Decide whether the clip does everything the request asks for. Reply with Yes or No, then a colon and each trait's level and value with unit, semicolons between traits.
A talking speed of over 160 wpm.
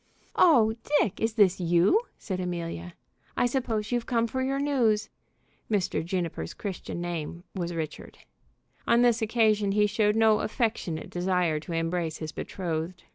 No: average, 145 wpm